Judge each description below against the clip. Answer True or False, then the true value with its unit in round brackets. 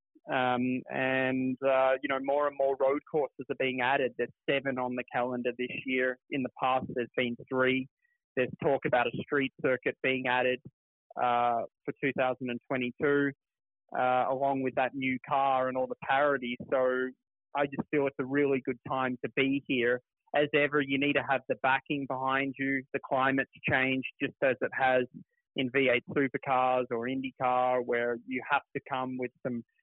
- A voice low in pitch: True (130 Hz)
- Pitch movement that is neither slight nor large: False (1.5 semitones)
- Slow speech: False (175 wpm)